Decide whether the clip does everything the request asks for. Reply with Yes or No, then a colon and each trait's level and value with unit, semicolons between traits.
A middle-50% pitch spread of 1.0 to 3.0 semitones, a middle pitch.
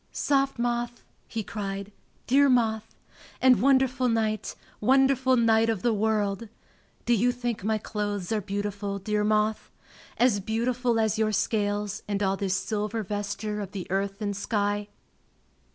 No: average, 2.7 semitones; high, 215 Hz